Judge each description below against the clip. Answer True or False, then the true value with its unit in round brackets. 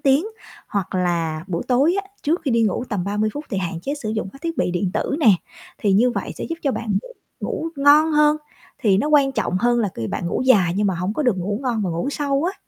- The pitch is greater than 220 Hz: True (230 Hz)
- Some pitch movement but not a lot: False (7.1 semitones)